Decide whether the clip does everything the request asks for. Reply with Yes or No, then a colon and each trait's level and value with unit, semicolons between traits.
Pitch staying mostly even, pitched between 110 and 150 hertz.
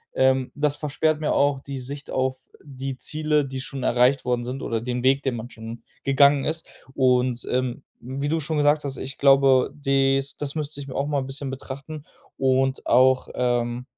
Yes: narrow, 1.8 semitones; low, 135 Hz